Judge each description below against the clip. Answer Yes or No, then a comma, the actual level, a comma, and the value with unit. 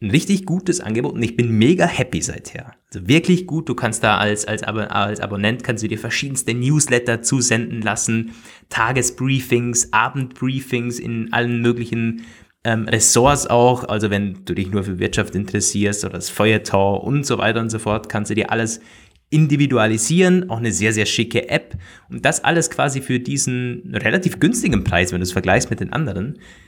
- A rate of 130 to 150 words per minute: No, average, 180 wpm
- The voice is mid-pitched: No, low, 115 Hz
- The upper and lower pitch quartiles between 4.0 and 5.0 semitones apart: No, average, 2.9 semitones